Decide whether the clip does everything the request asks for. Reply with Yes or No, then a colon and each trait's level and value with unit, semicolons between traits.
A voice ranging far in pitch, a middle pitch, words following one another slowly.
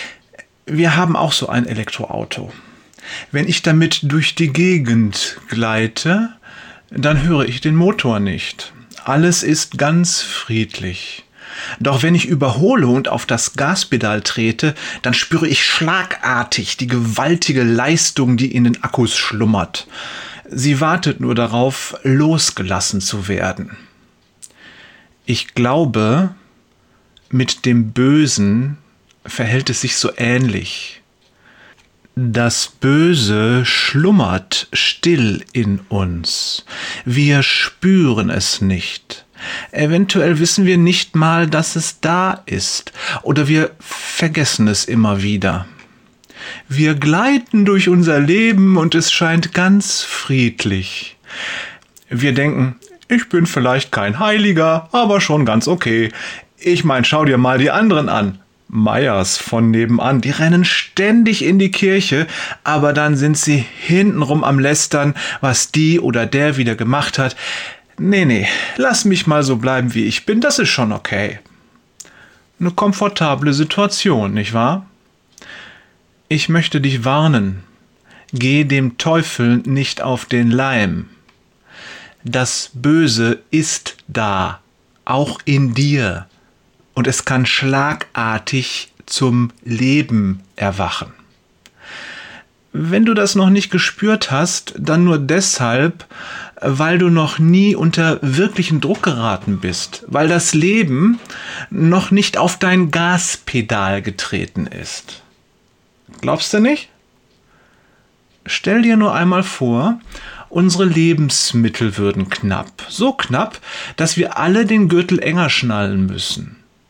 Yes: wide, 6.5 semitones; medium, 145 Hz; slow, 120 wpm